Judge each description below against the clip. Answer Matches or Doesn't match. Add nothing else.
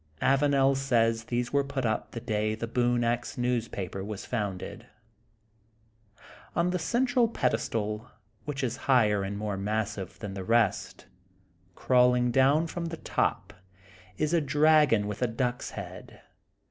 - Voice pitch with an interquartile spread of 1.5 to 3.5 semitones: Doesn't match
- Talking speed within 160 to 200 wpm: Doesn't match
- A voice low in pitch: Matches